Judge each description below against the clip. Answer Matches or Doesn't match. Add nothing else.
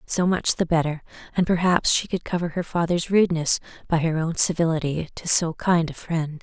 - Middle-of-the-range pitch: Matches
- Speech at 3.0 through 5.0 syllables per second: Doesn't match